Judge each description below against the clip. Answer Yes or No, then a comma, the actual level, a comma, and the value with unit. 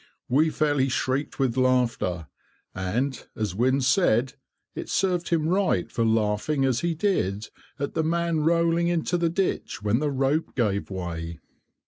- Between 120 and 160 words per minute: Yes, average, 150 wpm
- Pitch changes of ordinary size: No, wide, 6.7 semitones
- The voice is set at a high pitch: No, low, 135 Hz